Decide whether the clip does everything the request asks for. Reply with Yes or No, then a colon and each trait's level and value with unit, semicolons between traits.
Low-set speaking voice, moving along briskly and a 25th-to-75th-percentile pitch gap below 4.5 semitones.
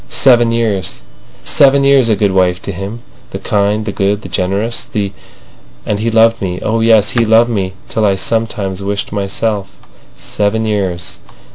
No: low, 105 Hz; average, 150 wpm; average, 2.7 semitones